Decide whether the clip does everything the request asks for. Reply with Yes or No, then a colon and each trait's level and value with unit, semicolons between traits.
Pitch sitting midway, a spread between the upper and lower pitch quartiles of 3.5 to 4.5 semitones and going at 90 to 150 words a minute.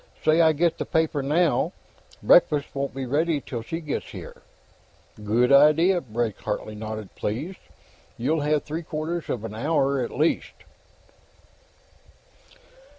No: medium, 145 Hz; average, 4.9 semitones; slow, 135 wpm